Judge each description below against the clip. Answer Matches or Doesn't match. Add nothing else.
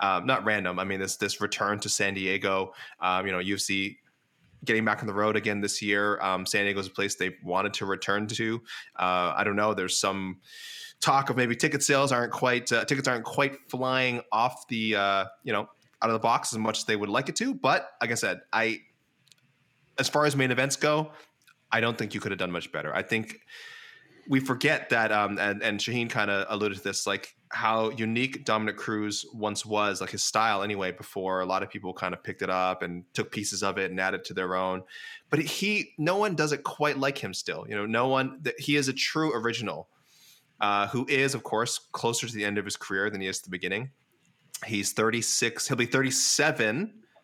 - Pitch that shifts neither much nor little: Matches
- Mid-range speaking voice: Doesn't match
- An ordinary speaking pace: Doesn't match